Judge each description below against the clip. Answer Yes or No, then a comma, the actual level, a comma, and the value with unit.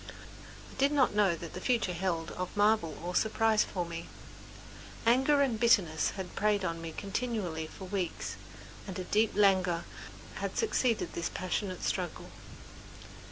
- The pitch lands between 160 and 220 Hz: Yes, high, 190 Hz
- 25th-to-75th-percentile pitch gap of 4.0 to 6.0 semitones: Yes, average, 4.5 semitones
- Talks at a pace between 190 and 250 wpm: No, average, 150 wpm